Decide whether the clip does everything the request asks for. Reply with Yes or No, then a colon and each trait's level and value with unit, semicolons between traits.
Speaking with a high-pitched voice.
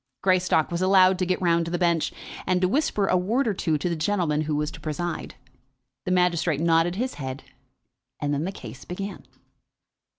No: medium, 175 Hz